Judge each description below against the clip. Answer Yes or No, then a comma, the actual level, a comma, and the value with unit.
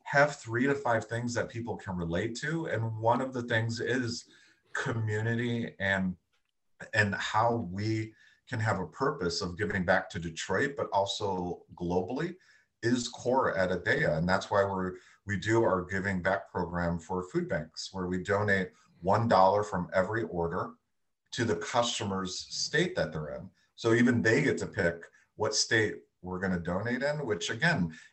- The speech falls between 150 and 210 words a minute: Yes, average, 170 wpm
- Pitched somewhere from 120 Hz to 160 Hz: No, low, 105 Hz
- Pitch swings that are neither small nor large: Yes, average, 4.3 semitones